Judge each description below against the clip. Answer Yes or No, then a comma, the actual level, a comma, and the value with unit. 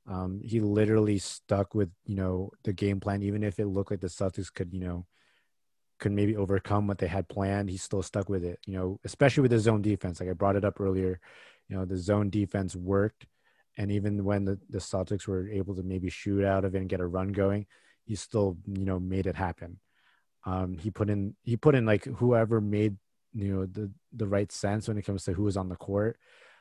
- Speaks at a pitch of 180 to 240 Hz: No, low, 100 Hz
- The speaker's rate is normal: No, fast, 230 wpm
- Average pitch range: No, narrow, 1.6 semitones